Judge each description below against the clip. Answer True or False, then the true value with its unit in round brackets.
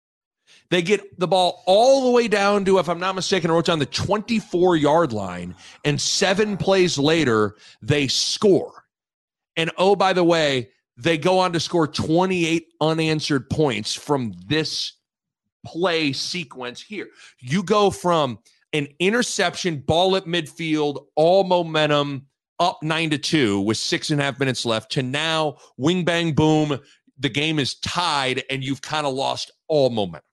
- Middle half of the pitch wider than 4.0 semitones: True (4.4 semitones)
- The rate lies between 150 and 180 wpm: True (160 wpm)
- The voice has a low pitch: False (160 Hz)